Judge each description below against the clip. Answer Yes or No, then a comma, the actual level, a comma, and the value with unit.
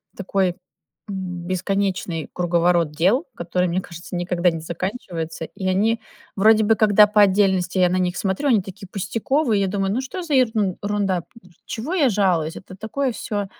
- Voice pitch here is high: Yes, high, 195 Hz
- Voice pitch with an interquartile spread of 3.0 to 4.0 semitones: Yes, average, 3.3 semitones